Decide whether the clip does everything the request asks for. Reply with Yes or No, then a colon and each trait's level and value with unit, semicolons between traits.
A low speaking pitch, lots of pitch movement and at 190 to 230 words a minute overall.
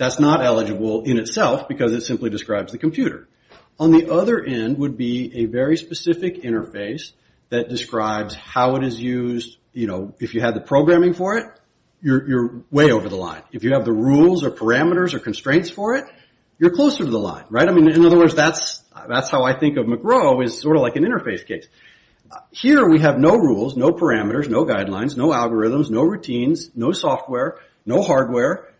Yes: low, 130 Hz; wide, 5.9 semitones; average, 200 wpm